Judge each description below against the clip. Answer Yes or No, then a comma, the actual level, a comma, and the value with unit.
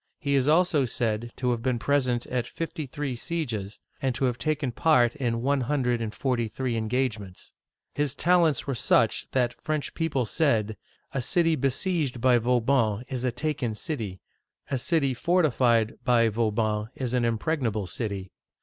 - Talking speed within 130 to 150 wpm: No, average, 165 wpm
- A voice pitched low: Yes, low, 125 Hz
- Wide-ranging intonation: No, average, 3.8 semitones